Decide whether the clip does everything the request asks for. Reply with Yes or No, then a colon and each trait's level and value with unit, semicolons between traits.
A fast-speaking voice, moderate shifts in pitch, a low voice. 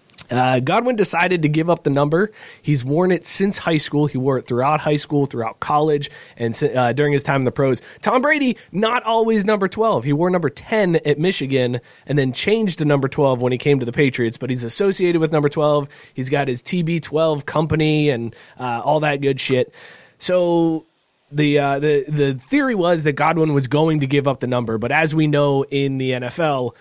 No: fast, 215 wpm; average, 3.7 semitones; medium, 150 Hz